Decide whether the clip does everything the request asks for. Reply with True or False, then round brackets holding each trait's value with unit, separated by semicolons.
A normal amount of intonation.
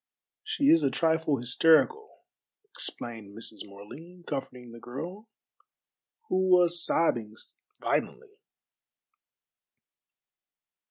False (7.1 semitones)